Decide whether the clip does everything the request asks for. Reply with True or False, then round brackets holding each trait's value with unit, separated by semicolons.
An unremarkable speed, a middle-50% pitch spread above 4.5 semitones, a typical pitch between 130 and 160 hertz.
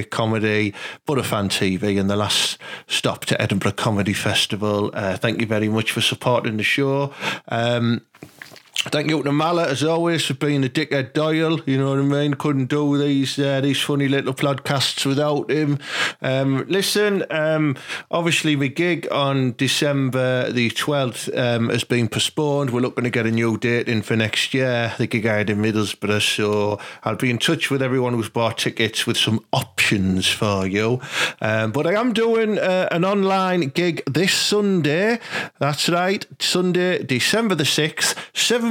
True (175 wpm; 5.1 semitones; 135 Hz)